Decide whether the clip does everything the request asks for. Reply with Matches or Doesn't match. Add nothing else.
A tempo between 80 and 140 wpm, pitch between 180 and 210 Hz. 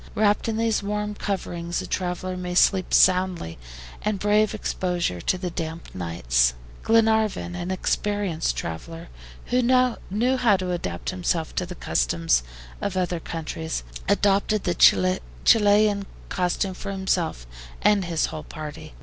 Matches